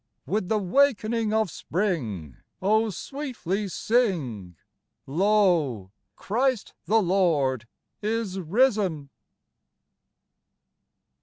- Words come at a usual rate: No, slow, 75 wpm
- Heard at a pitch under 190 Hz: No, high, 195 Hz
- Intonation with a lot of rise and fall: Yes, wide, 6.2 semitones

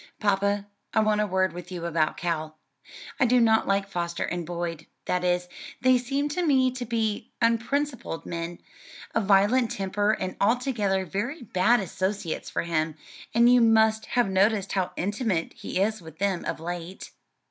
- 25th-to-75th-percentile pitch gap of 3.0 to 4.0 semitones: No, average, 4.6 semitones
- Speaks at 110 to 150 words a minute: No, average, 170 wpm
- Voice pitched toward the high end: Yes, high, 200 Hz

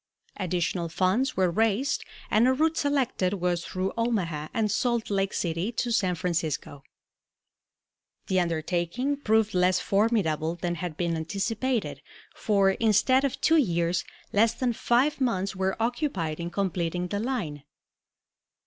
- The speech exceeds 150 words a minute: No, slow, 135 wpm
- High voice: Yes, high, 195 Hz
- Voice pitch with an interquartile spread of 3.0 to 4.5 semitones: No, average, 5.1 semitones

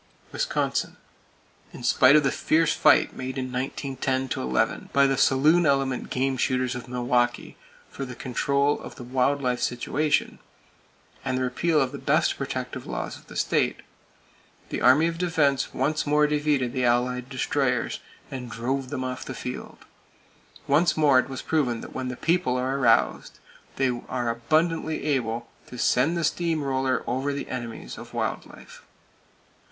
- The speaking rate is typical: Yes, average, 160 wpm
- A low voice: Yes, low, 130 Hz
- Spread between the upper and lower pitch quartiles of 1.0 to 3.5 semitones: Yes, narrow, 2.5 semitones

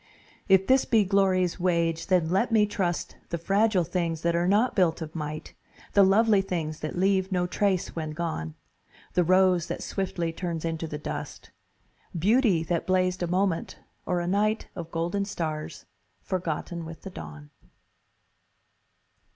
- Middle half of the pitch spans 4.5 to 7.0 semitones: No, average, 2.8 semitones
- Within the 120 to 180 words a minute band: Yes, average, 155 wpm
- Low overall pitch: No, medium, 180 Hz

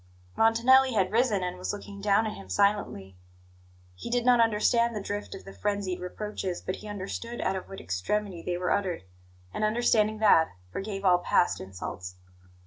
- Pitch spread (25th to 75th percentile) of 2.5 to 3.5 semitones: Yes, average, 3.2 semitones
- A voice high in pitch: Yes, high, 200 Hz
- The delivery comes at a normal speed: Yes, average, 175 wpm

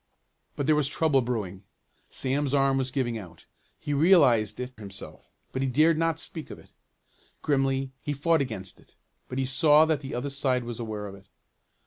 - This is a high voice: No, low, 135 Hz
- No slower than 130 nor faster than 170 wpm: No, average, 185 wpm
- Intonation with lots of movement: No, average, 3.7 semitones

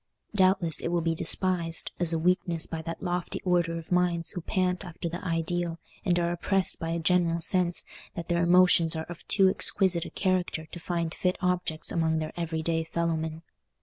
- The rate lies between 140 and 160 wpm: No, average, 185 wpm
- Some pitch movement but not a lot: No, narrow, 1.5 semitones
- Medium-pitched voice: Yes, medium, 170 Hz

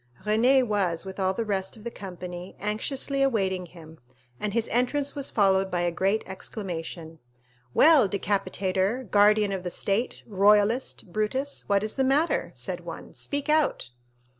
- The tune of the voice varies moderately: Yes, average, 4.2 semitones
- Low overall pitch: No, high, 205 Hz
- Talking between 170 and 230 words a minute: No, average, 155 wpm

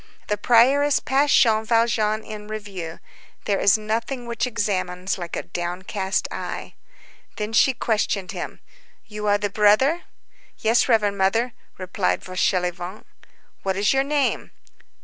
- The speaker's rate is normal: No, slow, 130 wpm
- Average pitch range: Yes, average, 3.4 semitones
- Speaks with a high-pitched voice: Yes, high, 210 Hz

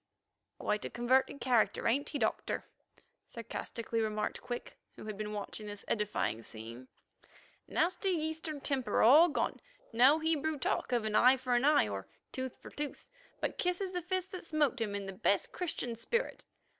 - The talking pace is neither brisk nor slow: Yes, average, 160 wpm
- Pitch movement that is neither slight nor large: No, wide, 6.6 semitones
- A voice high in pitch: Yes, very high, 255 Hz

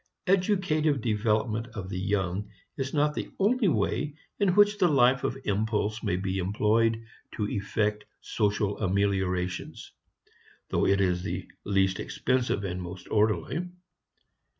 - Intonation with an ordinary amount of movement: No, wide, 5.9 semitones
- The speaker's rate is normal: No, slow, 130 wpm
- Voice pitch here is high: No, low, 105 Hz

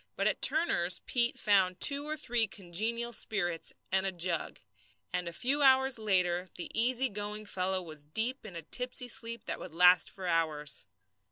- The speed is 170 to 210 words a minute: Yes, average, 175 wpm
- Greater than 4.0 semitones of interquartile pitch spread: Yes, average, 5.3 semitones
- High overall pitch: Yes, high, 195 Hz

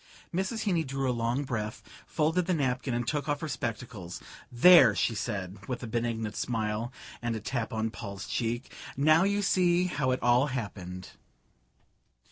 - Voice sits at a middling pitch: No, low, 120 Hz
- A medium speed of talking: Yes, average, 170 wpm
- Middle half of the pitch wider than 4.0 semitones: Yes, average, 4.9 semitones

